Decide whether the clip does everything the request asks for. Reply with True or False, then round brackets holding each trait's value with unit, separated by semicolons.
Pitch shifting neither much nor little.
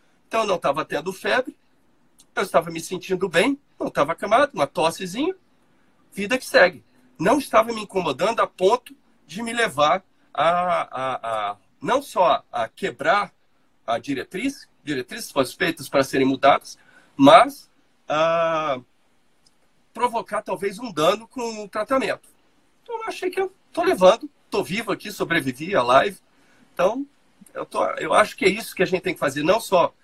False (7.1 semitones)